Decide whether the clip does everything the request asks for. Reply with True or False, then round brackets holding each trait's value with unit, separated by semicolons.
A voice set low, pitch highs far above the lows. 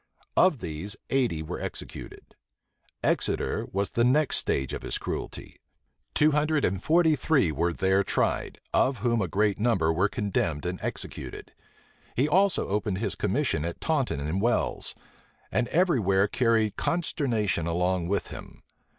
True (105 Hz; 7.0 semitones)